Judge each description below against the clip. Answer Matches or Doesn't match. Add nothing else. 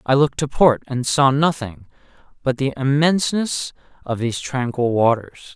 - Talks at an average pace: Matches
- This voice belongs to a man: Matches